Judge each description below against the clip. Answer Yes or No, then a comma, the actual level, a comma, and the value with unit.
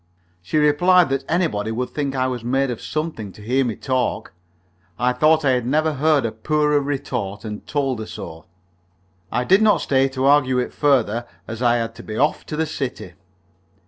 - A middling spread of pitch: Yes, average, 3.9 semitones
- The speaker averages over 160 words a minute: Yes, average, 195 wpm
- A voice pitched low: Yes, low, 130 Hz